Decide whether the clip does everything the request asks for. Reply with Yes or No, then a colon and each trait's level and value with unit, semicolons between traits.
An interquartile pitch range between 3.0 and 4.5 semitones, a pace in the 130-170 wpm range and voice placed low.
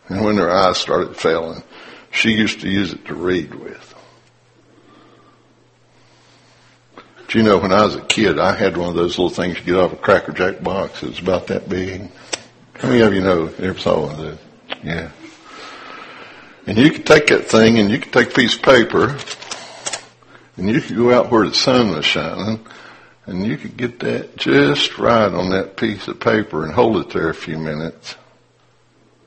No: average, 3.9 semitones; average, 195 wpm; very low, 95 Hz